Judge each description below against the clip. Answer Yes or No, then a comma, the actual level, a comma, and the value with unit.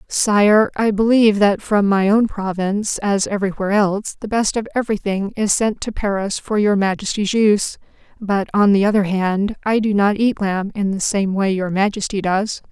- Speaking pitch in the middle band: No, high, 205 Hz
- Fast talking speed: No, average, 190 wpm